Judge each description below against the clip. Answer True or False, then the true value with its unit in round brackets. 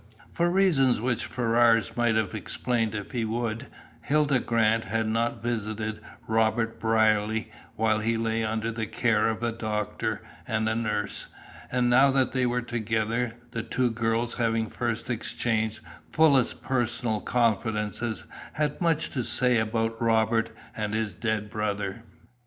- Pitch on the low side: True (115 Hz)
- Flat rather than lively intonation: True (1.7 semitones)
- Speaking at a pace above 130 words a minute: True (140 wpm)